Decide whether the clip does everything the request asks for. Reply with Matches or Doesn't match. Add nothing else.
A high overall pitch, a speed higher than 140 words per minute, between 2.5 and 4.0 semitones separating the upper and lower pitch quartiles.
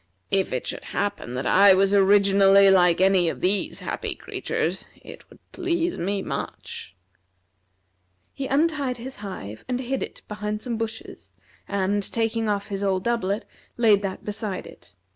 Matches